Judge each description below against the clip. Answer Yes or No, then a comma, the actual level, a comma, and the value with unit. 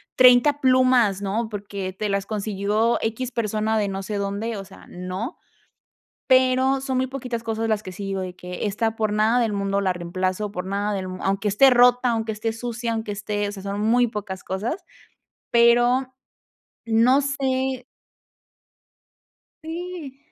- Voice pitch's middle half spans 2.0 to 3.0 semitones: No, average, 3.9 semitones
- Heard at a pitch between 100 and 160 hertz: No, high, 220 Hz